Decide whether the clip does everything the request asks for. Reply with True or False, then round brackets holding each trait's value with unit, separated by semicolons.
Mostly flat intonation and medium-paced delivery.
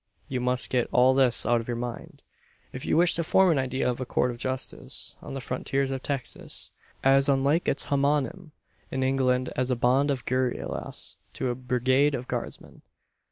True (1.6 semitones; 190 wpm)